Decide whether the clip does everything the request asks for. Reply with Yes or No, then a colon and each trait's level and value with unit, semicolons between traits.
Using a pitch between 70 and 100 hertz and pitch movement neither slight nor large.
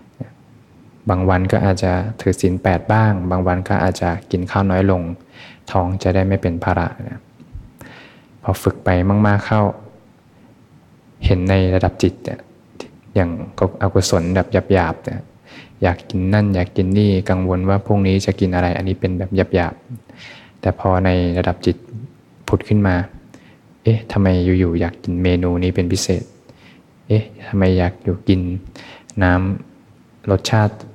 No: very low, 95 Hz; narrow, 2.0 semitones